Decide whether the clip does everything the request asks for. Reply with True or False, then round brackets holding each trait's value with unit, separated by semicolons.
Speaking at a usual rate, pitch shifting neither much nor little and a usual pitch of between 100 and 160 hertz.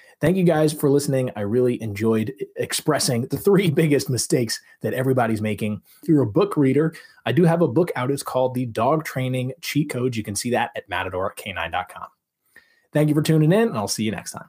False (210 wpm; 4.8 semitones; 135 Hz)